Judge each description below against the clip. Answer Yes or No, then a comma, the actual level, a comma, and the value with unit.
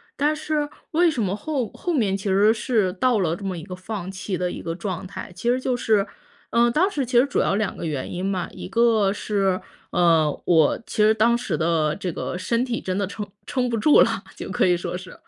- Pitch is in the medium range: No, high, 205 Hz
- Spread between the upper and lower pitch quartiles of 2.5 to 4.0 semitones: No, average, 4.7 semitones